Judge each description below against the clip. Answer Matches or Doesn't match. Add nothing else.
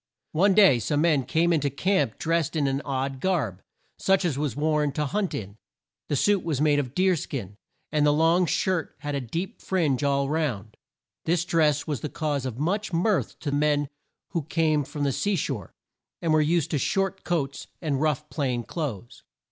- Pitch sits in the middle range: Matches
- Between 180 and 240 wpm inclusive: Matches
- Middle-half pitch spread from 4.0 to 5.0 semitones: Doesn't match